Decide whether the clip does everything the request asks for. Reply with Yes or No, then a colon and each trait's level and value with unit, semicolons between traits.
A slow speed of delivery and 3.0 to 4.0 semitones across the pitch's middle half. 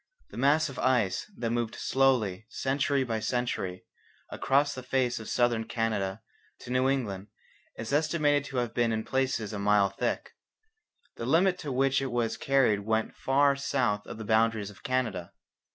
No: average, 170 wpm; average, 3.6 semitones